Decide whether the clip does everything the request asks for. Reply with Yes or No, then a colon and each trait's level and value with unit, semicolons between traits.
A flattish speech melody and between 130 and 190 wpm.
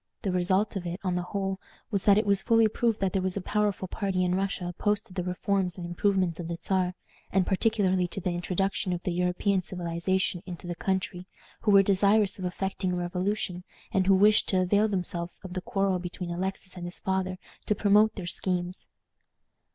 No: narrow, 1.8 semitones; fast, 205 wpm